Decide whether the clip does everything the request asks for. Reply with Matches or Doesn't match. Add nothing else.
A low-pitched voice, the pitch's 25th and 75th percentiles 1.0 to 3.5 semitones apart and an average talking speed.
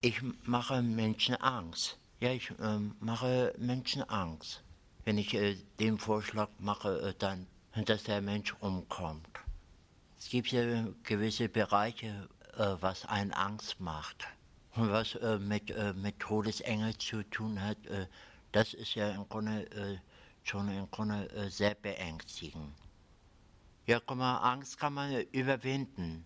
Matches